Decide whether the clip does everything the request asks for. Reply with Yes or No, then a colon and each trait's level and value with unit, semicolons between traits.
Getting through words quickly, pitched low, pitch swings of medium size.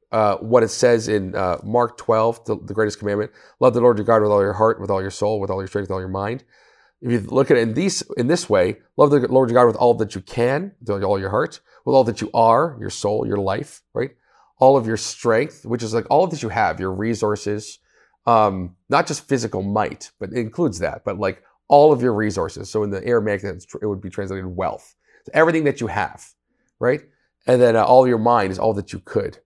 Yes: fast, 250 wpm; low, 110 Hz; average, 3.2 semitones